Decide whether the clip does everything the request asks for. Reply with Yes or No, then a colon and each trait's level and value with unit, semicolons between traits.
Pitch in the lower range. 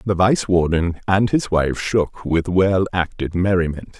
Yes: very low, 90 Hz